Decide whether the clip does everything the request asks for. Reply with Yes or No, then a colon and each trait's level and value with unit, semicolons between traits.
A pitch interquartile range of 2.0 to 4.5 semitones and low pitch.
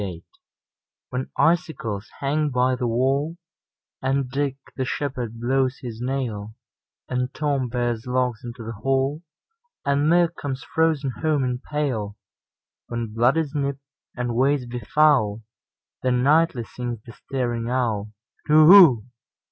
Yes: average, 3.5 semitones; low, 130 Hz